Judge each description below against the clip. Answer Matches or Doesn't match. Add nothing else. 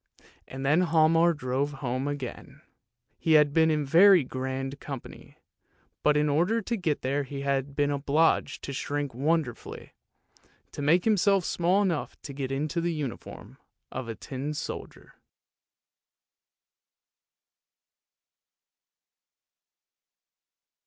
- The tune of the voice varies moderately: Matches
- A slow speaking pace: Matches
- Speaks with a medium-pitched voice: Matches